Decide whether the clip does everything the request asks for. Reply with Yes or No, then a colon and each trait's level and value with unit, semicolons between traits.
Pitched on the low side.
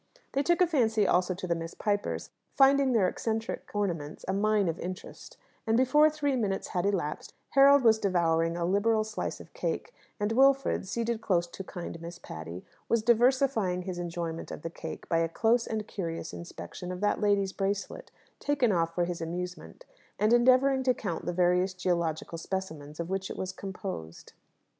No: high, 195 Hz